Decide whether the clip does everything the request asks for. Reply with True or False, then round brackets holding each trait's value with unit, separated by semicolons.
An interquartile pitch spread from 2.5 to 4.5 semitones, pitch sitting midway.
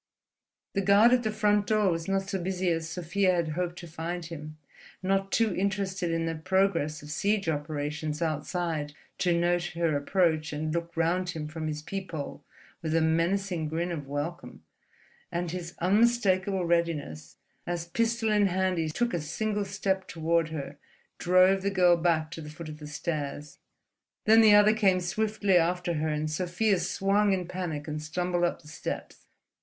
True (3.5 semitones; 175 Hz)